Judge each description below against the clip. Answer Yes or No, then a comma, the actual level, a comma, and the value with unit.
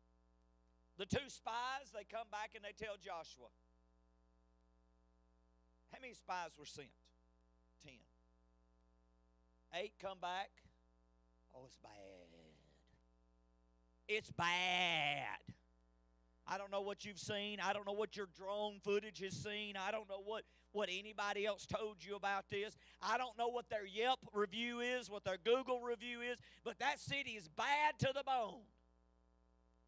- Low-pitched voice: No, medium, 180 Hz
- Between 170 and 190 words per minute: No, average, 145 wpm